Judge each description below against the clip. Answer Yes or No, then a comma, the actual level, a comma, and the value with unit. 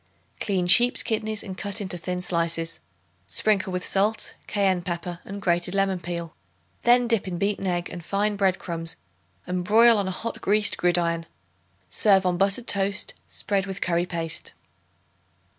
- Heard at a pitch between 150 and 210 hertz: Yes, high, 190 Hz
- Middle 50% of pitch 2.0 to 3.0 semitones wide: Yes, average, 2.7 semitones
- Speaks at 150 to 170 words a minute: Yes, average, 160 wpm